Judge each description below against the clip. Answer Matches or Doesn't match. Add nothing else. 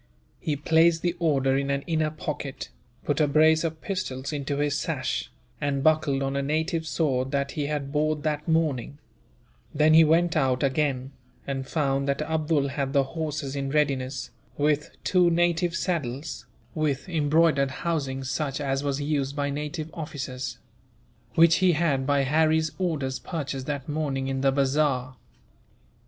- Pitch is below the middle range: Doesn't match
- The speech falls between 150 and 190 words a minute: Matches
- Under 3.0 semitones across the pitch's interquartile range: Matches